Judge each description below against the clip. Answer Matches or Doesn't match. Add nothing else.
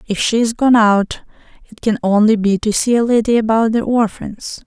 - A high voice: Matches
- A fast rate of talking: Doesn't match